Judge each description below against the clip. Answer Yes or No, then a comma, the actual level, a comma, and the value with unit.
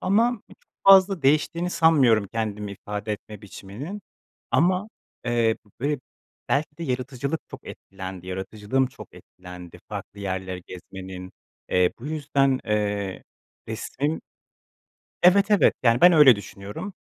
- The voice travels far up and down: Yes, wide, 7.7 semitones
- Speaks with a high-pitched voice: No, low, 120 Hz